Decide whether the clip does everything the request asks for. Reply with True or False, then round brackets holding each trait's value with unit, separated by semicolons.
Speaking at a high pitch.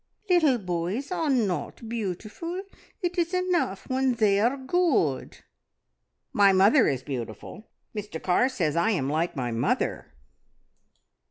True (215 Hz)